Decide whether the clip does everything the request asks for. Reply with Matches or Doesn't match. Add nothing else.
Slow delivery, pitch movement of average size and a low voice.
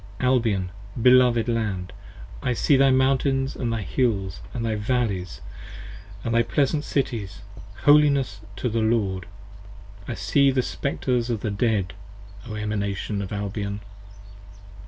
Matches